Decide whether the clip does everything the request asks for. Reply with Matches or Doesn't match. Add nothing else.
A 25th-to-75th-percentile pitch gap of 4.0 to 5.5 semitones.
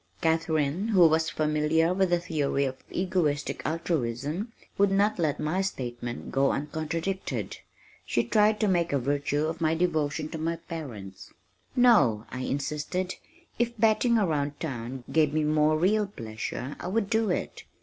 Matches